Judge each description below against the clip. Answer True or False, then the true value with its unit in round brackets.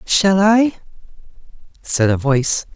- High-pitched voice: False (175 Hz)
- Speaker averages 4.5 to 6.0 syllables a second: False (3.9 syllables/s)